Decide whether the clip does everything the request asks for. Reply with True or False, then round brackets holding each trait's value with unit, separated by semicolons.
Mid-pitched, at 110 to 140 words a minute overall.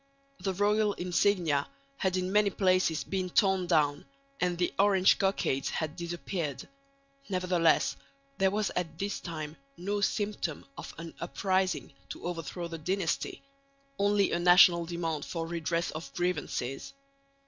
True (180 Hz; 135 wpm)